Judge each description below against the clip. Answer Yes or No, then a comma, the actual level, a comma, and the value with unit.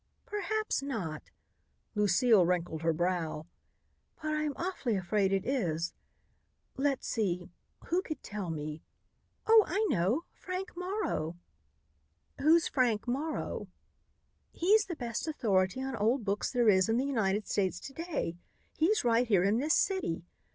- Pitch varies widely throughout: Yes, wide, 8.8 semitones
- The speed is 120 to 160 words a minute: Yes, average, 140 wpm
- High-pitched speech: Yes, high, 230 Hz